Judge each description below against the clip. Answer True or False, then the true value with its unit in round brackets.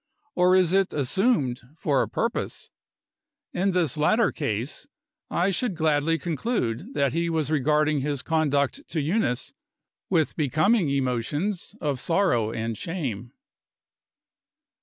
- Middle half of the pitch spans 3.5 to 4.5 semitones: False (5.0 semitones)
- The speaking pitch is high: False (155 Hz)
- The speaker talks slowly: True (120 wpm)